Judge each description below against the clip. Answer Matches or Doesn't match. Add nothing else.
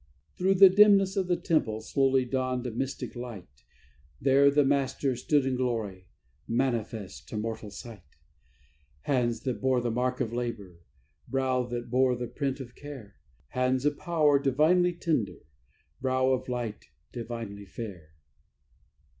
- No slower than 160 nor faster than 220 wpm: Doesn't match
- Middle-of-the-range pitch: Doesn't match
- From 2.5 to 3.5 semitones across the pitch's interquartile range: Matches